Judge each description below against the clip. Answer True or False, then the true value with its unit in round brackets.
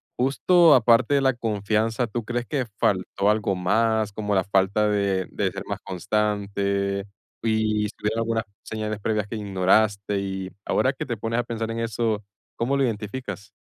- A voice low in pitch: True (110 Hz)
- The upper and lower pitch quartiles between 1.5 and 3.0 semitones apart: True (2.4 semitones)